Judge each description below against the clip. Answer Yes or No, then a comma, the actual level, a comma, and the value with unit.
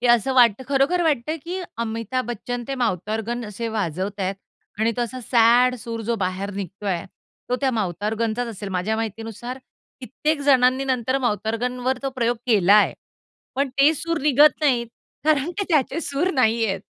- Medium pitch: No, high, 240 Hz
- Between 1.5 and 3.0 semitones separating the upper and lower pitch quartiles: No, average, 3.5 semitones